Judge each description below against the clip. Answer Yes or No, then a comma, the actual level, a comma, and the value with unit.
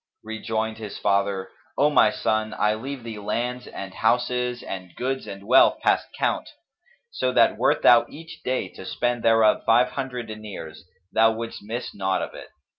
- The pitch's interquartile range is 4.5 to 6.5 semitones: No, average, 3.1 semitones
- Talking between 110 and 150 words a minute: No, average, 170 wpm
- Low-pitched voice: Yes, low, 110 Hz